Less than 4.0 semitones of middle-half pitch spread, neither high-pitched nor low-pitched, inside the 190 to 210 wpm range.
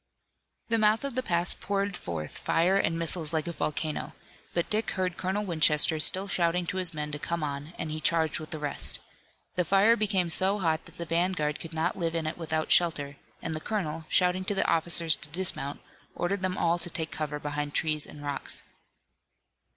Yes: average, 3.2 semitones; medium, 165 Hz; average, 200 wpm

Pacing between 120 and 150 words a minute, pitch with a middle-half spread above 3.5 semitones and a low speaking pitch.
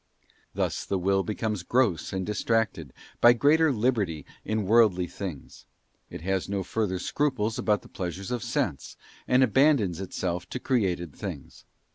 Yes: average, 145 wpm; average, 4.6 semitones; low, 100 Hz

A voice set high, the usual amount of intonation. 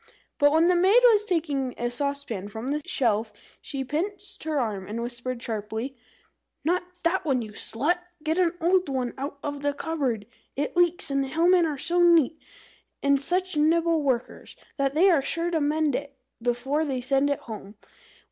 Yes: very high, 285 Hz; average, 4.9 semitones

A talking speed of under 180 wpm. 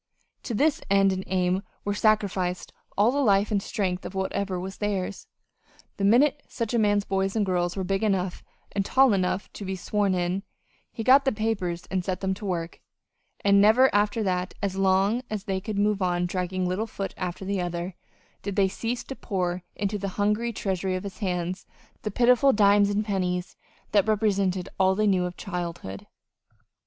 No: average, 190 wpm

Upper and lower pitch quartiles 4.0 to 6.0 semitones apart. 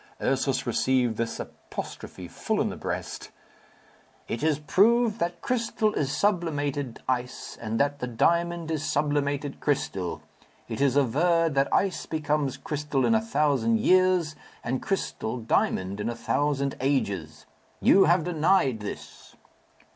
Yes: average, 5.1 semitones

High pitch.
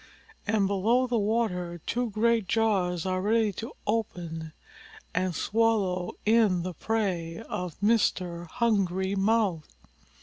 Yes: high, 200 Hz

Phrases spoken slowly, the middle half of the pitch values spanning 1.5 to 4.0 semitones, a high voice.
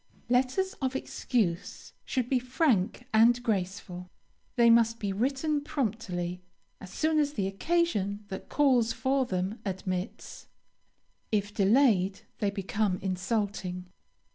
No: slow, 115 wpm; average, 5.0 semitones; high, 220 Hz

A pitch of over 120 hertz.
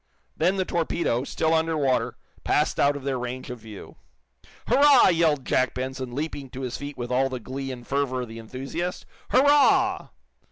Yes: low, 135 Hz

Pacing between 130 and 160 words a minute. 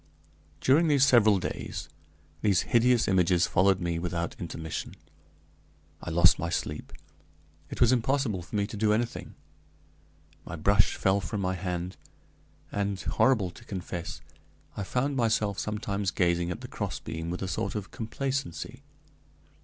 Yes: average, 140 wpm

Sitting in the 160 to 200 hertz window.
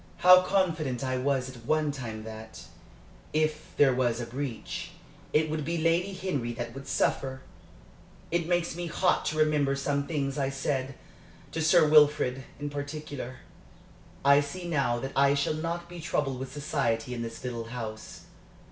No: medium, 140 Hz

